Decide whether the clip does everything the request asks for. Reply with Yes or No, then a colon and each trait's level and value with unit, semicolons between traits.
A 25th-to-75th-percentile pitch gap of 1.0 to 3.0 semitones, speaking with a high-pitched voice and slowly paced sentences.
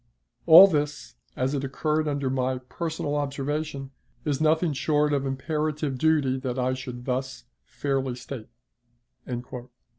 No: narrow, 2.6 semitones; medium, 140 Hz; slow, 130 wpm